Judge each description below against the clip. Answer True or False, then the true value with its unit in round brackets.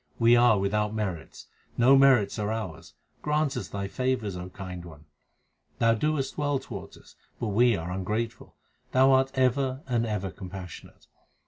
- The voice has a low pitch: True (115 Hz)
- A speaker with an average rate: True (155 wpm)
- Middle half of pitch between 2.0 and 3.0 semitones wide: False (5.1 semitones)